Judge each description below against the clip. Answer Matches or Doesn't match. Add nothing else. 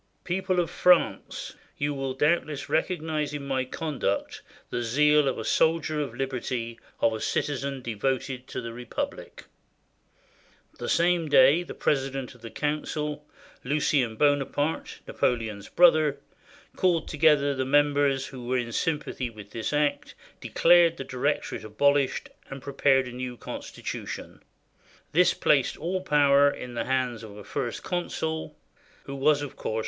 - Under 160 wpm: Matches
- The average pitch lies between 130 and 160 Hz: Matches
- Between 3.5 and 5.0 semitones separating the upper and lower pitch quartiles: Doesn't match